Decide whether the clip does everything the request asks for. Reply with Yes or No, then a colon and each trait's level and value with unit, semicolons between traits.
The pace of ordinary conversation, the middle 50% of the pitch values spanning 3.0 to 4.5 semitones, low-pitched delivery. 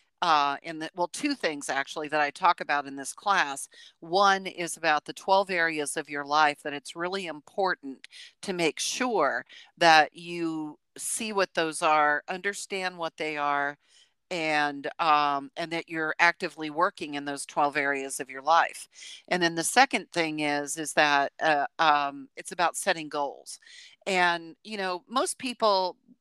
No: average, 165 wpm; average, 3.7 semitones; medium, 165 Hz